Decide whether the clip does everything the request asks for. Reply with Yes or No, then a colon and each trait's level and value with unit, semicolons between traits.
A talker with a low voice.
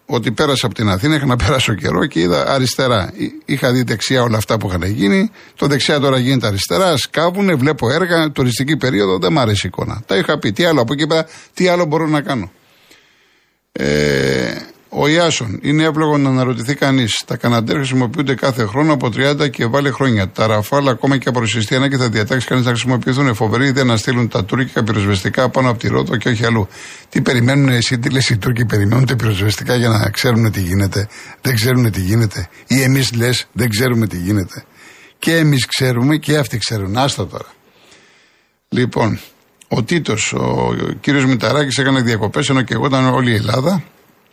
Yes: low, 125 Hz